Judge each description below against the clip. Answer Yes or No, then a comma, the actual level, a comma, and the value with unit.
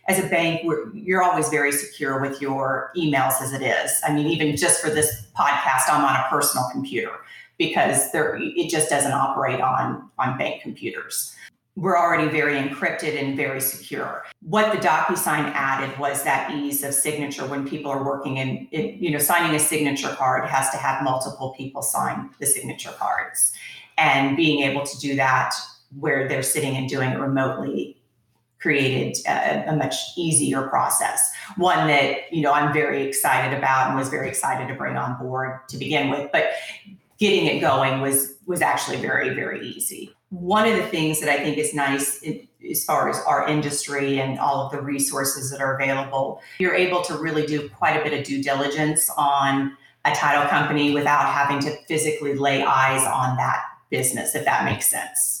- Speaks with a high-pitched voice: No, medium, 140 Hz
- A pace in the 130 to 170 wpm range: No, average, 185 wpm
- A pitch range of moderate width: No, narrow, 2.1 semitones